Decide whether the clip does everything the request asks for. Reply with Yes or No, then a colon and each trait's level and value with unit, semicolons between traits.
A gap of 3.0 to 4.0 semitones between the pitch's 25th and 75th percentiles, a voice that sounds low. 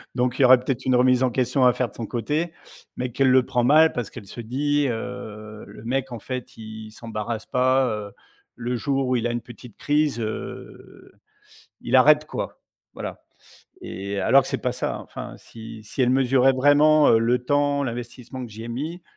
No: narrow, 2.6 semitones; low, 125 Hz